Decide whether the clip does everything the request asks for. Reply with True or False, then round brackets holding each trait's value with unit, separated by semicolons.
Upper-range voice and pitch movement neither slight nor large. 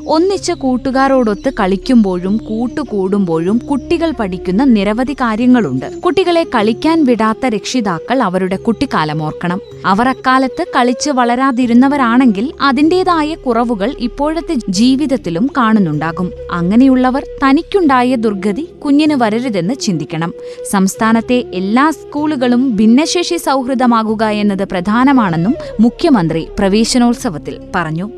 True (245 Hz; 5.0 semitones)